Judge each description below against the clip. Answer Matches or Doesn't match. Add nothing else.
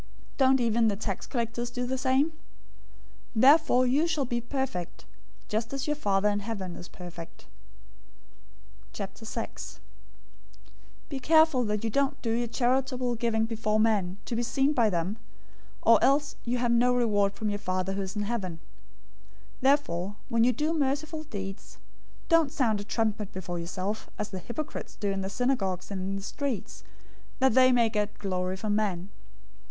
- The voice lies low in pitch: Doesn't match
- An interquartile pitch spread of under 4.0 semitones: Doesn't match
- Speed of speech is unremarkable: Matches